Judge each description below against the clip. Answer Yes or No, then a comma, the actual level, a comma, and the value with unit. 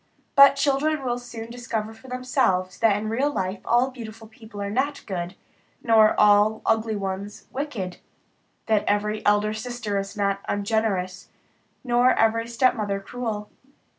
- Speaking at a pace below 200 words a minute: Yes, average, 140 wpm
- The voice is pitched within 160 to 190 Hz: No, high, 220 Hz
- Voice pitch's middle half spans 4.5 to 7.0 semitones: No, average, 3.1 semitones